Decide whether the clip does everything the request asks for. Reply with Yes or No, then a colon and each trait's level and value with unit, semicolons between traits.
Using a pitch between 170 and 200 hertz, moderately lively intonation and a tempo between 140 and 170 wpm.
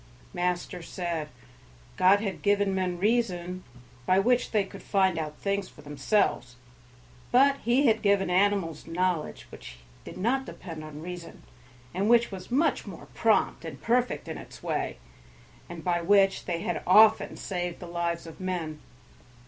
Yes: medium, 185 Hz; average, 3.0 semitones; average, 155 wpm